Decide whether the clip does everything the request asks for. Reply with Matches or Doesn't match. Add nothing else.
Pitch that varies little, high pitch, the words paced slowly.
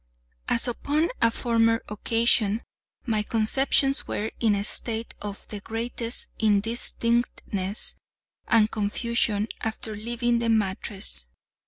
Matches